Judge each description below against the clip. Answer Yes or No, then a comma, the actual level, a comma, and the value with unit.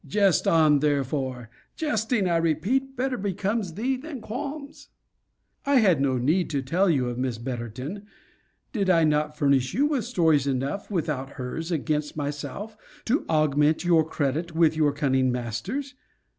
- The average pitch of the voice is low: No, medium, 160 Hz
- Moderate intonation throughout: No, wide, 6.8 semitones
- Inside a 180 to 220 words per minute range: No, average, 150 wpm